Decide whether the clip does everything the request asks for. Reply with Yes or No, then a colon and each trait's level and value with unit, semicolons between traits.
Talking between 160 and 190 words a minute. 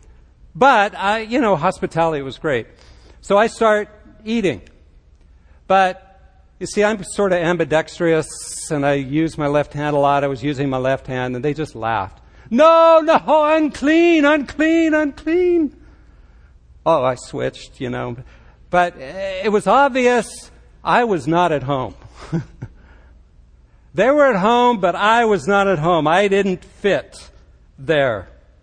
No: average, 145 wpm